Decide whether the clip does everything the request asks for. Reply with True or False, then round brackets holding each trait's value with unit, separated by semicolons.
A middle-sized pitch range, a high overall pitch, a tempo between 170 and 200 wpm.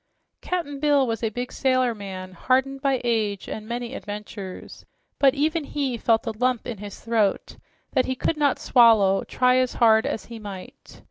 True (3.7 semitones; 240 Hz; 180 wpm)